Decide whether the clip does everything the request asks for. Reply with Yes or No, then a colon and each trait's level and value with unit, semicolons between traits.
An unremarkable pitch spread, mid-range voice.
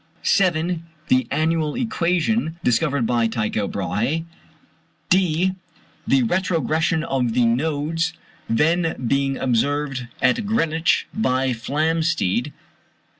Yes: average, 4.5 semitones; medium, 155 Hz